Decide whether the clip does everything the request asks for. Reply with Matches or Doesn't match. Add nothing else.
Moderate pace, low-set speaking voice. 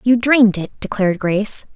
Doesn't match